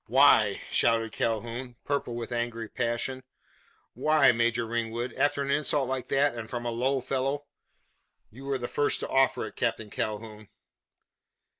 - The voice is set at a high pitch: No, low, 120 Hz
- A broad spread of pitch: No, average, 2.7 semitones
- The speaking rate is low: No, average, 155 wpm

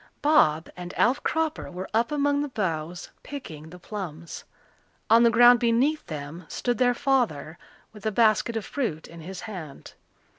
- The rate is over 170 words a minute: No, average, 160 wpm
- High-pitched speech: Yes, high, 215 Hz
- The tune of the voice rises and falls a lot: Yes, wide, 6.8 semitones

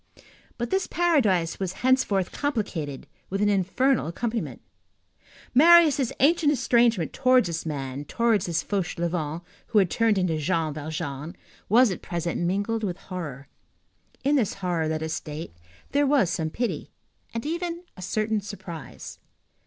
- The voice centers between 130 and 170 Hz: No, high, 195 Hz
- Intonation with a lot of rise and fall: Yes, wide, 6.9 semitones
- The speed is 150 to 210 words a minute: No, average, 140 wpm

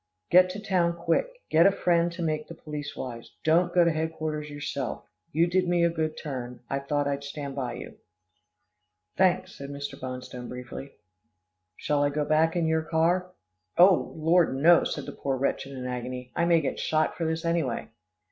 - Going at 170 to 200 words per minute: Yes, average, 190 wpm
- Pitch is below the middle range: No, medium, 155 Hz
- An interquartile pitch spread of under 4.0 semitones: Yes, average, 3.5 semitones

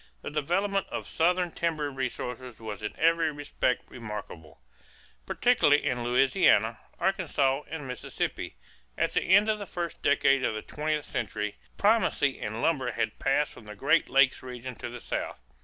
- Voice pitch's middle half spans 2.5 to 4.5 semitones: No, wide, 5.4 semitones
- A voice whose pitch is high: No, medium, 140 Hz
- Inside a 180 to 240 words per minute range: No, average, 155 wpm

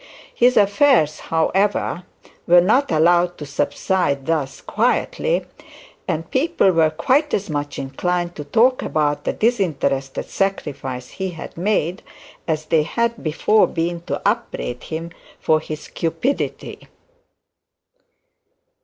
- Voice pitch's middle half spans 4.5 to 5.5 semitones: Yes, average, 5.0 semitones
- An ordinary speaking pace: No, slow, 120 wpm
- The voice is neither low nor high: Yes, medium, 170 Hz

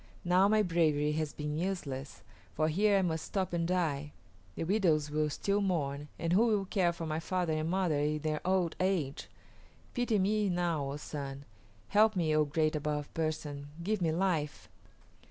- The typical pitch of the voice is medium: Yes, medium, 165 Hz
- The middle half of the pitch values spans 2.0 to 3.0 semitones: No, average, 3.8 semitones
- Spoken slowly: No, average, 175 wpm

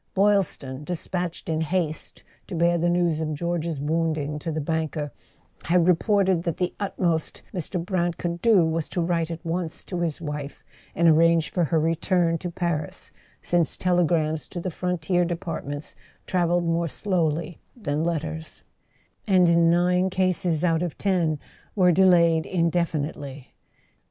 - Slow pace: No, average, 150 wpm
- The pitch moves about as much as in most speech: No, narrow, 1.9 semitones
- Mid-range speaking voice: Yes, medium, 170 Hz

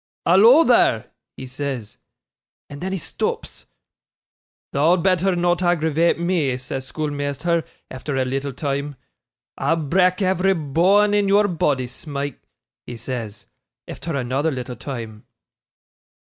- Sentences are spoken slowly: Yes, slow, 120 wpm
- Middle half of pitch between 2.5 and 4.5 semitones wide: No, average, 5.2 semitones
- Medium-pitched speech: Yes, medium, 150 Hz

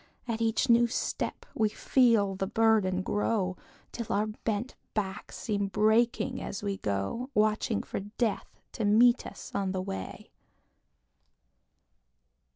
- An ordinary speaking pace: No, slow, 130 wpm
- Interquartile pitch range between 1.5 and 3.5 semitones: Yes, average, 2.7 semitones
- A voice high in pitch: Yes, high, 215 Hz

